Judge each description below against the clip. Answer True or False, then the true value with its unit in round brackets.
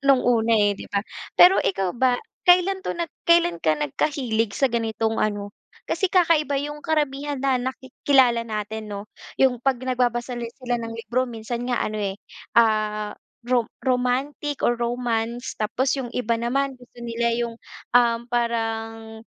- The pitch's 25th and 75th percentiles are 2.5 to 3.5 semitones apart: True (2.9 semitones)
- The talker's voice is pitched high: True (240 Hz)